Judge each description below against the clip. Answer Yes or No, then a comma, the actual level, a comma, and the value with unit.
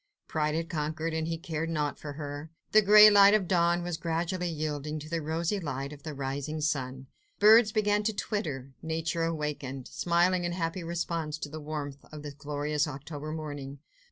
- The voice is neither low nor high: Yes, medium, 155 Hz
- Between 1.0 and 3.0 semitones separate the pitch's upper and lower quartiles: Yes, average, 2.7 semitones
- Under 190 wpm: Yes, average, 180 wpm